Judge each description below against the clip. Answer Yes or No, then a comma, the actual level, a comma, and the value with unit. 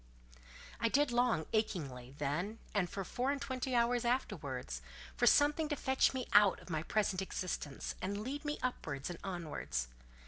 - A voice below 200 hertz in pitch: No, high, 205 Hz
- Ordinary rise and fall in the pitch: No, wide, 8.1 semitones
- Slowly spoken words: No, average, 165 wpm